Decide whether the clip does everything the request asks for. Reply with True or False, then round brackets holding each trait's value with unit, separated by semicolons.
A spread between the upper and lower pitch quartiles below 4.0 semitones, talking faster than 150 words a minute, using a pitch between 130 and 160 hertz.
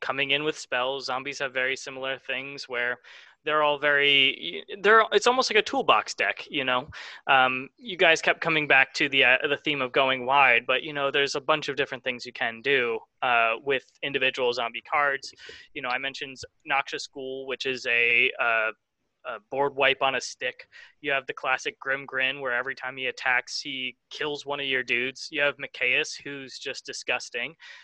True (2.6 semitones; 200 wpm; 140 Hz)